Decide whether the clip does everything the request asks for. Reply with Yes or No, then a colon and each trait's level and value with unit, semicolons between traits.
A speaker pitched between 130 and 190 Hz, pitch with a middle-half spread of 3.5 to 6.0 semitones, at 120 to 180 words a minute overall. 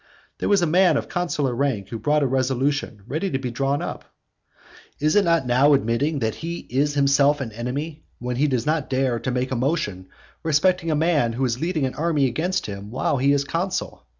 No: medium, 140 Hz; average, 3.9 semitones; fast, 205 wpm